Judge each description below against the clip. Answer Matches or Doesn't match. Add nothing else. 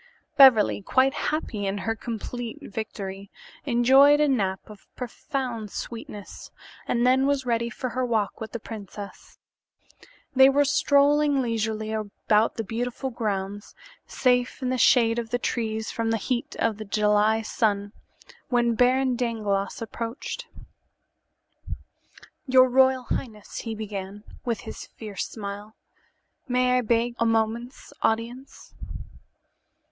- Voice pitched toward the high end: Matches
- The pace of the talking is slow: Matches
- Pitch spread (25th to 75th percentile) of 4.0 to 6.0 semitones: Doesn't match